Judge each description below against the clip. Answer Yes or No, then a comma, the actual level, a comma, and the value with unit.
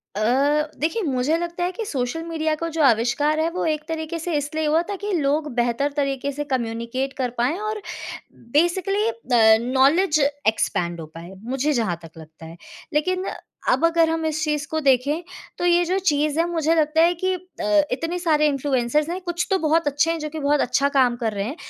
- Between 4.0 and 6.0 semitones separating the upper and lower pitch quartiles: Yes, average, 4.4 semitones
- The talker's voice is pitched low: No, very high, 300 Hz